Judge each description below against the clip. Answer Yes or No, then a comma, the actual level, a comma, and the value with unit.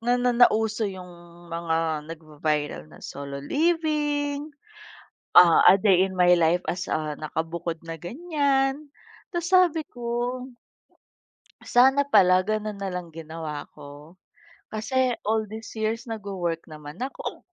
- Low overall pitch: No, high, 195 Hz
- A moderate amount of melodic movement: No, wide, 7.3 semitones